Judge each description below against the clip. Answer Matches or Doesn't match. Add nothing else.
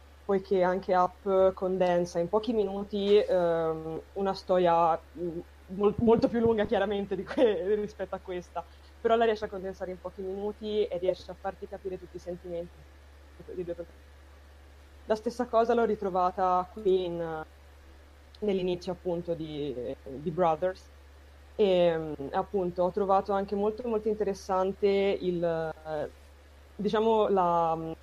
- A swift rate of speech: Doesn't match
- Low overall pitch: Doesn't match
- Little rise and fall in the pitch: Doesn't match